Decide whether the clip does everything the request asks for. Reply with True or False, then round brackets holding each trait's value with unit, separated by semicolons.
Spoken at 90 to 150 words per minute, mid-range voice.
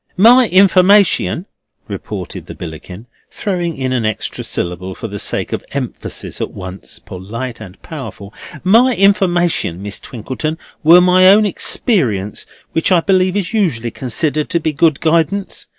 True (140 wpm; 160 Hz)